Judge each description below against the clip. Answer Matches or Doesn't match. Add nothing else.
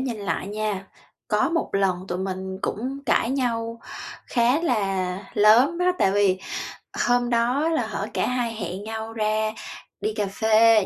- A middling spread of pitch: Matches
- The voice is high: Matches